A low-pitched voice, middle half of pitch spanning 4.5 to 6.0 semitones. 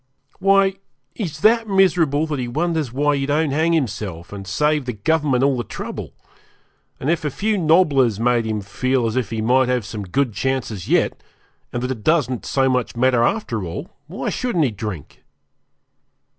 Yes: low, 130 Hz; wide, 5.5 semitones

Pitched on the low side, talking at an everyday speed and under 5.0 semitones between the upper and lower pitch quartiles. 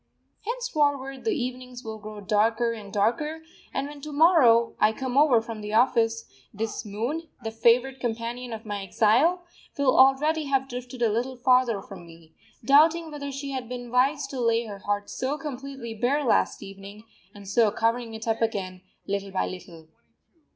No: high, 240 Hz; average, 170 wpm; average, 4.1 semitones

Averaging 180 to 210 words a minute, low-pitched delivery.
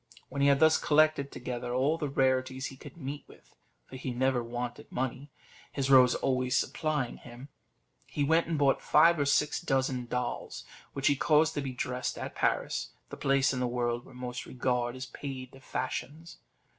Yes: average, 190 wpm; low, 130 Hz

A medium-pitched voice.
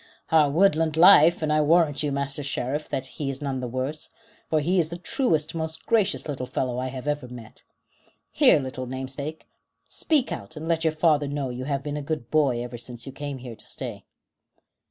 Yes: medium, 145 Hz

